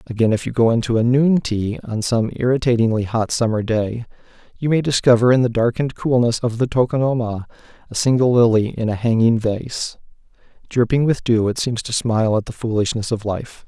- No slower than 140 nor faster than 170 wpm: No, average, 190 wpm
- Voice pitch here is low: Yes, low, 120 Hz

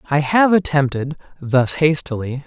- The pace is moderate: No, slow, 120 wpm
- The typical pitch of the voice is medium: Yes, medium, 145 Hz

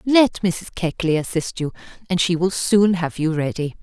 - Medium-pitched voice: Yes, medium, 175 Hz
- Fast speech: No, average, 190 wpm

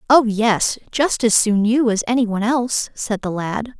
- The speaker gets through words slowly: No, fast, 205 wpm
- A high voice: Yes, high, 225 Hz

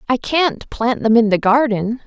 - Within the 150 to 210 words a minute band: Yes, fast, 205 wpm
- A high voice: Yes, high, 235 Hz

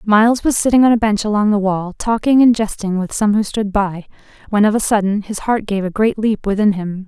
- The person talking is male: No, female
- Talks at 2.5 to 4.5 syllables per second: No, 5.6 syllables/s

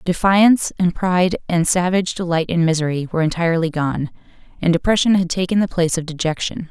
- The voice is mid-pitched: Yes, medium, 175 Hz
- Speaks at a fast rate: No, average, 170 wpm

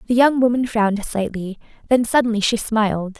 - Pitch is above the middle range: Yes, high, 220 Hz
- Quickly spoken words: No, average, 170 wpm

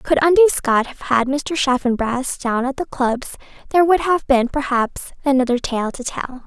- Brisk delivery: No, average, 185 wpm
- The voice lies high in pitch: Yes, very high, 270 Hz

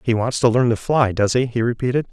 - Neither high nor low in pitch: No, low, 120 Hz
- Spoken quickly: Yes, fast, 285 wpm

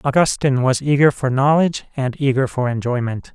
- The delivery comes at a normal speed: Yes, average, 160 wpm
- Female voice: No, male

